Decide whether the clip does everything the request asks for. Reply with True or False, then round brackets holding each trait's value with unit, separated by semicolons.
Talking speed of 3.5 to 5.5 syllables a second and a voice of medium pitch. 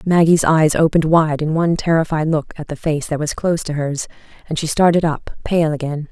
False (5.7 syllables/s; 155 Hz)